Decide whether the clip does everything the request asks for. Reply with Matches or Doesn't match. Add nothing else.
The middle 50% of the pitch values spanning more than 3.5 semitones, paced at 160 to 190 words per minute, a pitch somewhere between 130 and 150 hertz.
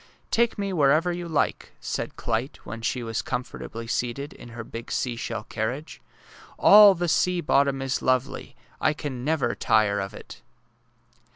Matches